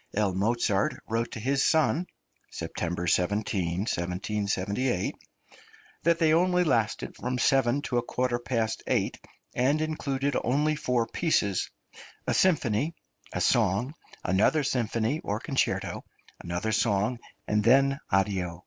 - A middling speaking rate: No, slow, 120 wpm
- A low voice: Yes, low, 120 Hz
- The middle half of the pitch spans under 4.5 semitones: No, average, 5.2 semitones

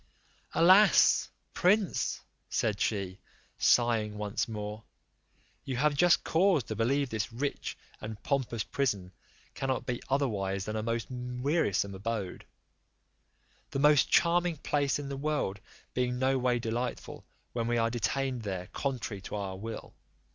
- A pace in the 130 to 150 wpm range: Yes, slow, 135 wpm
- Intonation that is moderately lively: Yes, average, 4.5 semitones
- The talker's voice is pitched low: Yes, low, 120 Hz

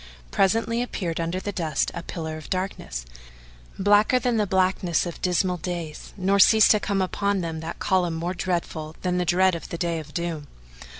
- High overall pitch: No, medium, 180 Hz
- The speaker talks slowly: No, average, 185 wpm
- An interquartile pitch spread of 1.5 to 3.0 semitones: Yes, average, 2.7 semitones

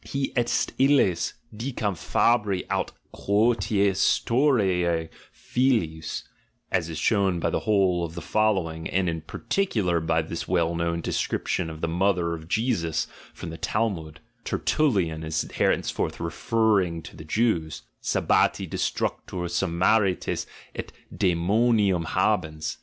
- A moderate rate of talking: No, slow, 125 wpm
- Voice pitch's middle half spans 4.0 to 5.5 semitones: Yes, average, 4.7 semitones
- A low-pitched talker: Yes, very low, 90 Hz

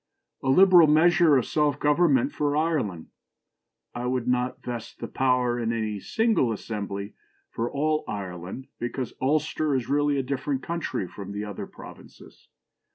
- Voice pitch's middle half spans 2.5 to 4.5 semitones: No, average, 4.9 semitones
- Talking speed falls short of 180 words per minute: Yes, average, 155 wpm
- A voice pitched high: No, low, 130 Hz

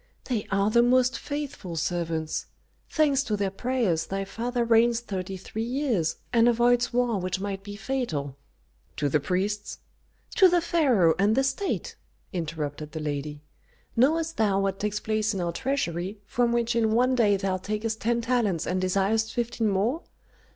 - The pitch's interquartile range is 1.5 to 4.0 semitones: No, average, 4.6 semitones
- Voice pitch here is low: No, high, 215 Hz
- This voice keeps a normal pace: Yes, average, 165 wpm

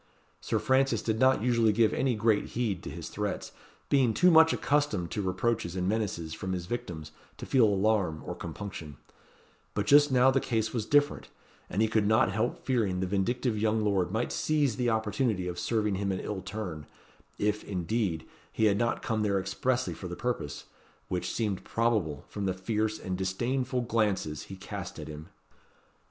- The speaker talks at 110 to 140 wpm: No, average, 180 wpm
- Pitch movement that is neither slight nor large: Yes, average, 4.1 semitones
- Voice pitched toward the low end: Yes, low, 110 Hz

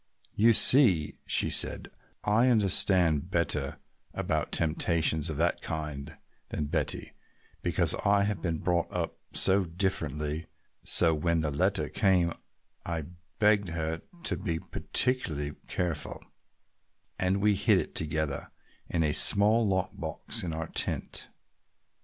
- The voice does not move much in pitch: No, average, 4.0 semitones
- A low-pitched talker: Yes, very low, 85 Hz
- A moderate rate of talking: No, slow, 130 wpm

